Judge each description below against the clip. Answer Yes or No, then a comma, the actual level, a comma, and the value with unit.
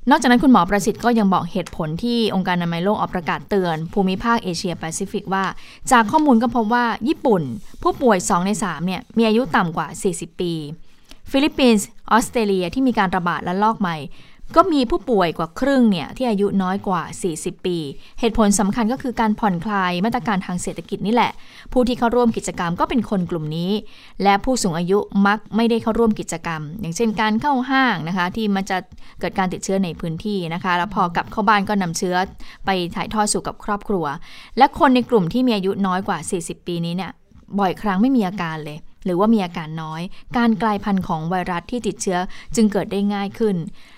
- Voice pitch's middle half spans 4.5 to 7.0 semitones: No, average, 4.1 semitones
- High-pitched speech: Yes, high, 200 Hz